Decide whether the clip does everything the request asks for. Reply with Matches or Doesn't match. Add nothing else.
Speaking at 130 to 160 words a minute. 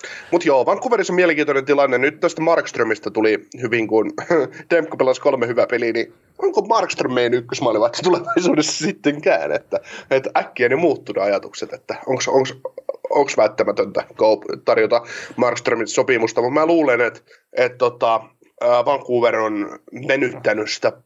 Matches